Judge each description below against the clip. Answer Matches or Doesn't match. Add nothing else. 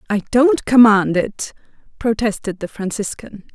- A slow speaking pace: Matches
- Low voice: Doesn't match